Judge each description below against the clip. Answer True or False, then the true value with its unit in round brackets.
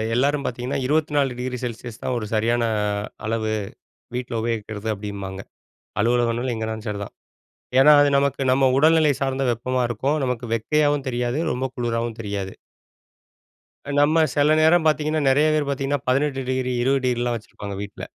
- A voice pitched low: True (125 Hz)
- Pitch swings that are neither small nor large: True (3.6 semitones)